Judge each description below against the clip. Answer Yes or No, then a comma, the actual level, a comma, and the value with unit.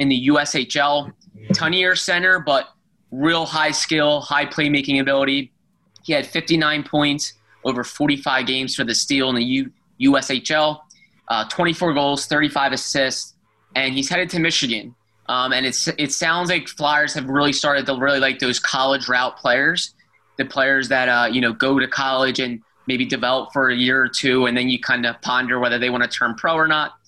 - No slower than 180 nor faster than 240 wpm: Yes, average, 185 wpm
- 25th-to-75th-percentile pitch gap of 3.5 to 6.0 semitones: No, average, 2.8 semitones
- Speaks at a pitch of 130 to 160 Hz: Yes, medium, 140 Hz